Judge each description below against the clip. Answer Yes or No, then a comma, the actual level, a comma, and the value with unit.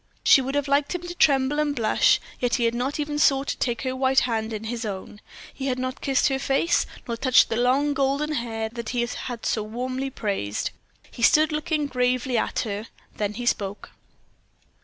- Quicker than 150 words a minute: Yes, average, 200 wpm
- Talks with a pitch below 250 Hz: No, very high, 255 Hz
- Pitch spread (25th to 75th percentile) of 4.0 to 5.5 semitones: No, average, 3.3 semitones